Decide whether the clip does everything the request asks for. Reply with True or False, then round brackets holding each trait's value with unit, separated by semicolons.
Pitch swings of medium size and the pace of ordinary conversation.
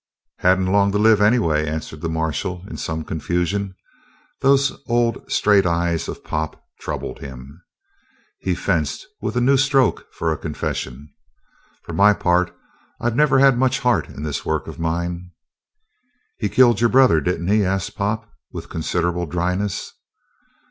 False (5.7 semitones; 155 wpm)